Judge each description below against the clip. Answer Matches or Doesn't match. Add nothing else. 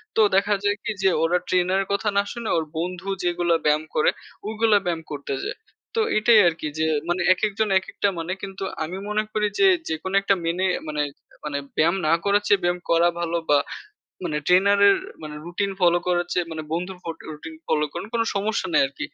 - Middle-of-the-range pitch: Matches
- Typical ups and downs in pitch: Matches